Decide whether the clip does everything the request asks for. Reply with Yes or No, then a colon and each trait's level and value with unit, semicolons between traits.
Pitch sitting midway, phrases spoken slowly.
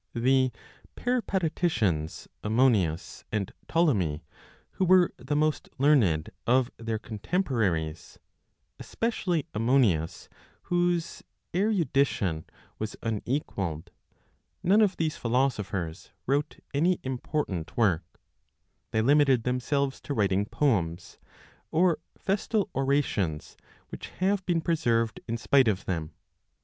No: low, 130 Hz; slow, 100 wpm